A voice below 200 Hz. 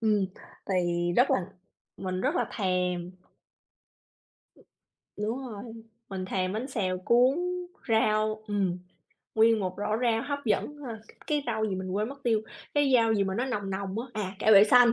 No: high, 215 Hz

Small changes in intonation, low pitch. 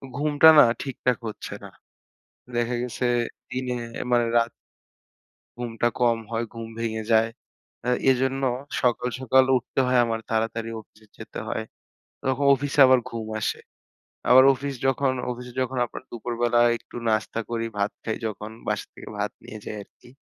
Yes: narrow, 2.3 semitones; low, 120 Hz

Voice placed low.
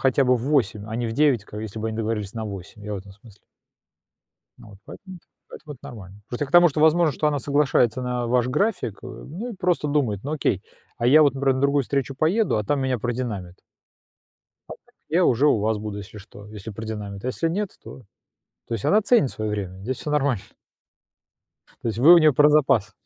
Yes: low, 125 Hz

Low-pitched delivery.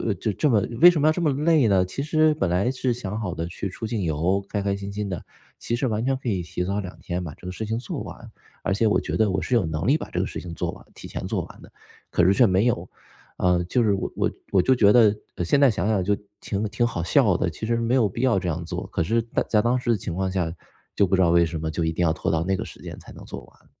Yes: low, 100 Hz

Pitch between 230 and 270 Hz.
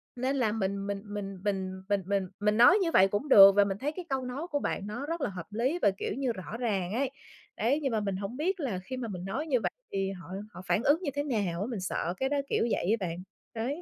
No: high, 215 Hz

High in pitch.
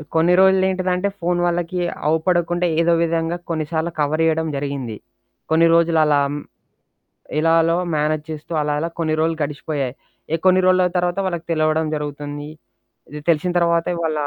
No: medium, 165 Hz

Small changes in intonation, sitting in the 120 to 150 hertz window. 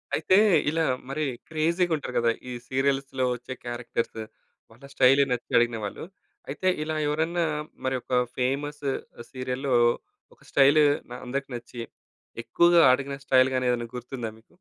No: average, 3.2 semitones; low, 135 Hz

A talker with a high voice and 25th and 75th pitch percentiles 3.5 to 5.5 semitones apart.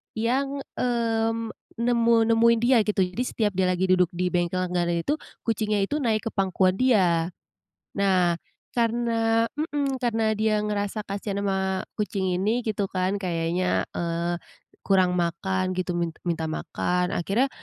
Yes: high, 200 Hz; average, 4.1 semitones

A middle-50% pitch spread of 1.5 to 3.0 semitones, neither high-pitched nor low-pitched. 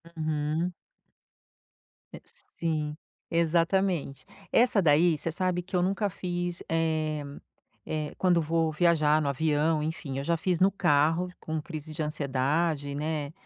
Yes: narrow, 2.6 semitones; medium, 160 Hz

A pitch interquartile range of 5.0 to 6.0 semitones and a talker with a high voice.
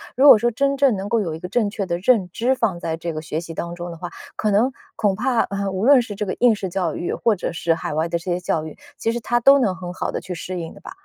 Yes: wide, 5.4 semitones; high, 195 Hz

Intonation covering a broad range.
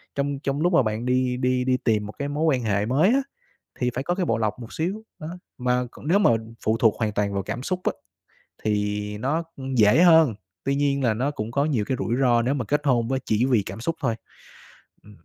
No: average, 4.7 semitones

